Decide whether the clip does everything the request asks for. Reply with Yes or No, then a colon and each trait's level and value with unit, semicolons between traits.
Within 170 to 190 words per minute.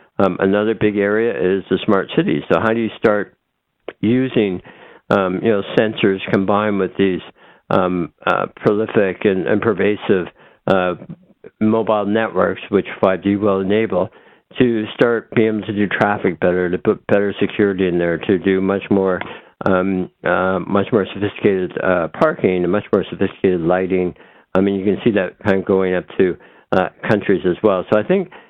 Yes: average, 175 wpm